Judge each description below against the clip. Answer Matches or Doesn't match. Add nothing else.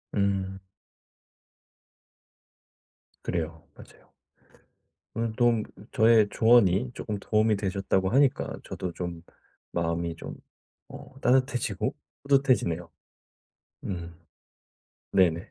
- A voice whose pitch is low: Matches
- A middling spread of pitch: Matches